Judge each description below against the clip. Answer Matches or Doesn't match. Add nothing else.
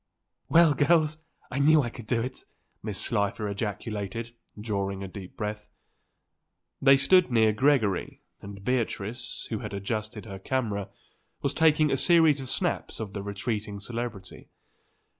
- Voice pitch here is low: Matches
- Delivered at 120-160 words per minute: Matches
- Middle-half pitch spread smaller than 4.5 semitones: Doesn't match